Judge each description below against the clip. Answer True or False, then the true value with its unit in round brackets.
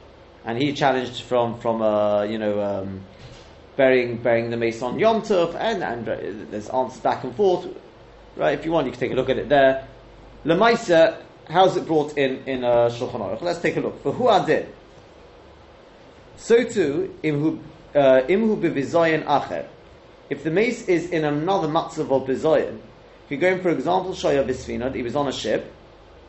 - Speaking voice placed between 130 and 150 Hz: True (135 Hz)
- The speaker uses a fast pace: False (170 wpm)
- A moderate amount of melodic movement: False (6.1 semitones)